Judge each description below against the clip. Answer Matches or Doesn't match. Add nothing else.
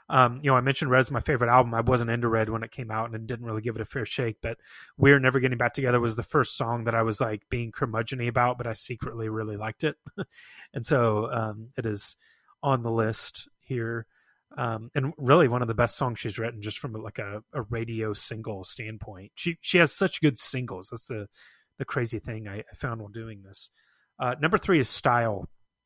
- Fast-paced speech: Matches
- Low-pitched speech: Matches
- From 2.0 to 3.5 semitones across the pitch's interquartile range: Matches